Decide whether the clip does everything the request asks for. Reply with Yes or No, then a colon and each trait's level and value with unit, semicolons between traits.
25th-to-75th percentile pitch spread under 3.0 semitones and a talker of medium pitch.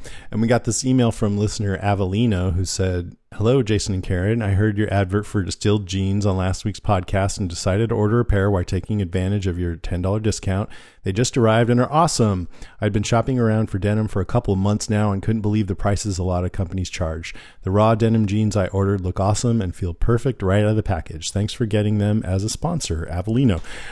No: narrow, 2.6 semitones; low, 105 Hz